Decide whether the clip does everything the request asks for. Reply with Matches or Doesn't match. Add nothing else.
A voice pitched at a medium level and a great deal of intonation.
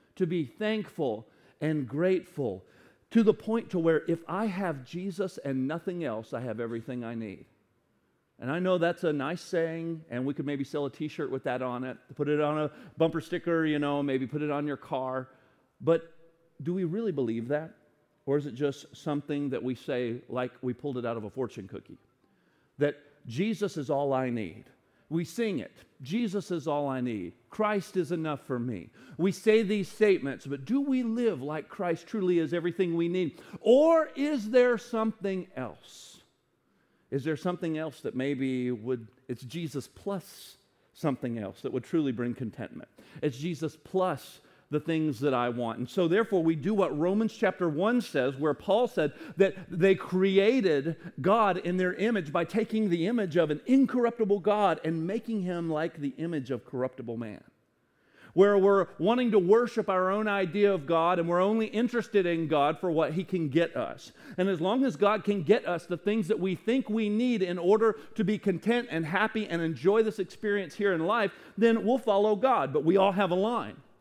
Matches